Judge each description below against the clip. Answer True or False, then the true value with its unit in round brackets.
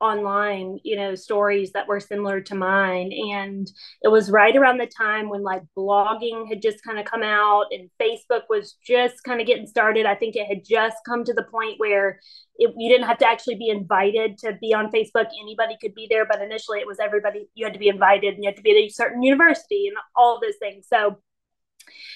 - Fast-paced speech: True (230 wpm)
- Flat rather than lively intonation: True (2.3 semitones)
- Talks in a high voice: True (215 Hz)